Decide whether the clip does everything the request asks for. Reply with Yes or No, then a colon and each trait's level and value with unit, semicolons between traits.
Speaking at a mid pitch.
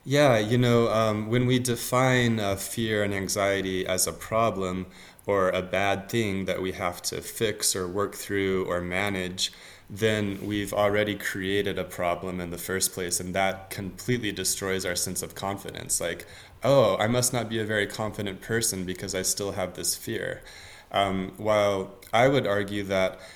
No: low, 100 Hz